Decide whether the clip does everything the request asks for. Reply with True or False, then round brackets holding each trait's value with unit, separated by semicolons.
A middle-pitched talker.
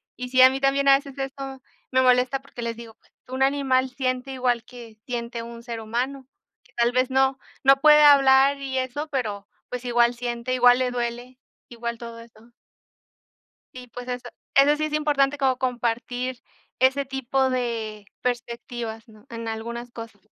False (250 Hz)